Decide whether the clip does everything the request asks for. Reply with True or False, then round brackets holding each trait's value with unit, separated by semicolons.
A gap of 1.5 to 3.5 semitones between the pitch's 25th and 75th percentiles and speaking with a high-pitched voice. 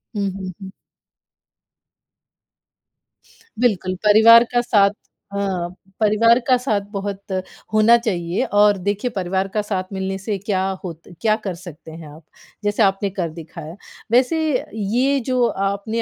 True (2.9 semitones; 200 Hz)